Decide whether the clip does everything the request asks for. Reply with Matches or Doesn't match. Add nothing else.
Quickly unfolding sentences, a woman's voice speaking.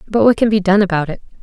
Matches